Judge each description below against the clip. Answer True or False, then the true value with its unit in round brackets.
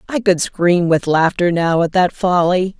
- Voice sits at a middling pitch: True (175 Hz)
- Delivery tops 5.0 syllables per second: False (4.2 syllables/s)